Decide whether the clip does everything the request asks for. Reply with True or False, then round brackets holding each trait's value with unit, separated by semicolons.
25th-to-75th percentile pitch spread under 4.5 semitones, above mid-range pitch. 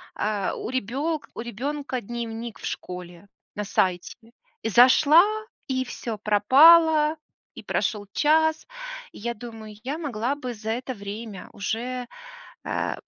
False (5.0 semitones; 240 Hz)